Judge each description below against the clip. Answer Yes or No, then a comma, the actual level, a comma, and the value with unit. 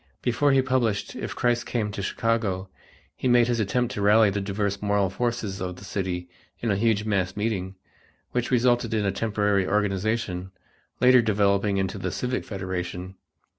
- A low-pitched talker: Yes, low, 105 Hz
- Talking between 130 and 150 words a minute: No, average, 170 wpm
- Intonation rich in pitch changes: No, average, 3.2 semitones